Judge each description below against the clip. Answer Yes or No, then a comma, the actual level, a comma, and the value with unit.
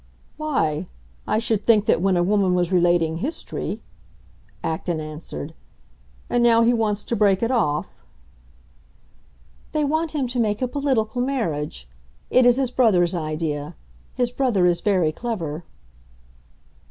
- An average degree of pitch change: No, wide, 6.4 semitones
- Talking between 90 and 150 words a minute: Yes, average, 140 wpm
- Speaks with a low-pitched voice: No, high, 205 Hz